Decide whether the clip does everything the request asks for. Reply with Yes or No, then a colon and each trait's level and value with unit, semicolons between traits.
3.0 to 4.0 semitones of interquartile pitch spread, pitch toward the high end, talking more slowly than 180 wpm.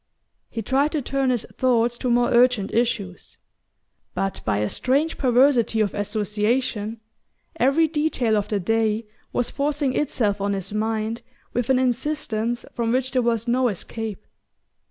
Yes: average, 3.3 semitones; high, 235 Hz; average, 150 wpm